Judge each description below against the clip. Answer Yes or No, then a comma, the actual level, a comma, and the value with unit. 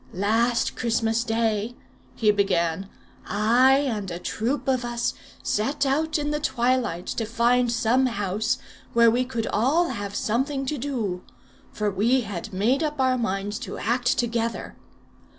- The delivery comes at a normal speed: Yes, average, 150 wpm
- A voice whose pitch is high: Yes, high, 235 Hz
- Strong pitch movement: No, average, 3.4 semitones